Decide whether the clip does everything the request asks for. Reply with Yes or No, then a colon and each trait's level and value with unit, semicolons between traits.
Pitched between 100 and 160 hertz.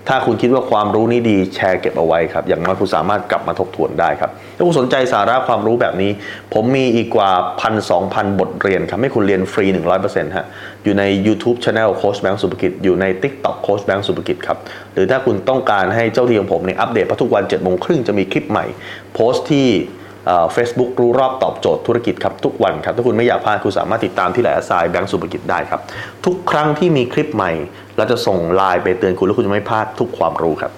Yes: low, 110 Hz